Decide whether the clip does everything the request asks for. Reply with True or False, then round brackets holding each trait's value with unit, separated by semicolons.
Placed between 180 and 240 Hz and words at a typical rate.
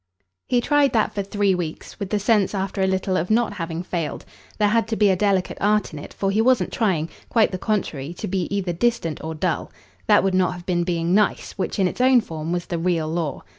False (190 Hz; 240 wpm)